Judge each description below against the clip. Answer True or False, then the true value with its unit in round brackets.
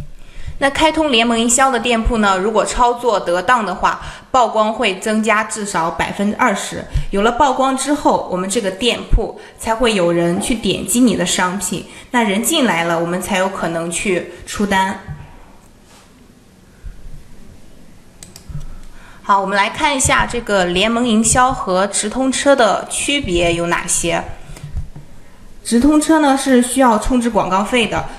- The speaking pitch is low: False (220 Hz)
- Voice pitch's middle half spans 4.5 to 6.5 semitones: True (5.1 semitones)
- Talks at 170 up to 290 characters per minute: True (220 characters per minute)